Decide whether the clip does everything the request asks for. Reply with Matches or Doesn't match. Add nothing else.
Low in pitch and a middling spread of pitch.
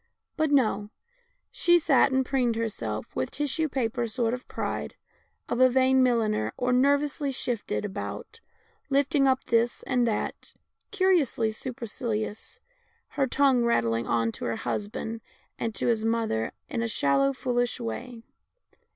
Doesn't match